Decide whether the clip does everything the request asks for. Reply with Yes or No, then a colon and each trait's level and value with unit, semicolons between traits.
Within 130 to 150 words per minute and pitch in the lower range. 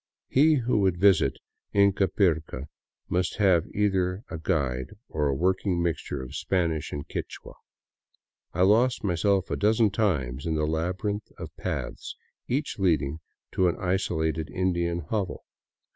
Yes: slow, 135 wpm; very low, 90 Hz